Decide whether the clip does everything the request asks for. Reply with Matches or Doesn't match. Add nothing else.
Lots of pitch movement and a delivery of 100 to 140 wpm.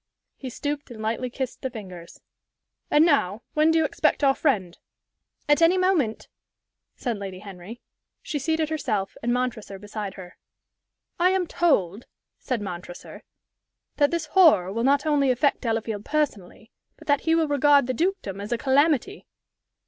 Doesn't match